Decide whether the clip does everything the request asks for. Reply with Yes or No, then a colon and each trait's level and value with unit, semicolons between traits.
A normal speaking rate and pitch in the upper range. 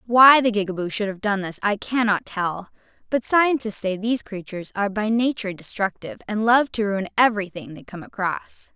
Yes: average, 190 wpm; high, 210 Hz